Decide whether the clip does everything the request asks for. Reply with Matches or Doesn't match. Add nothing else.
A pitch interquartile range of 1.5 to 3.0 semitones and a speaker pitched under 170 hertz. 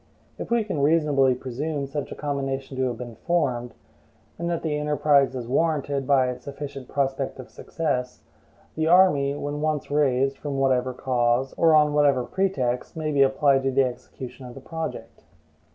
Matches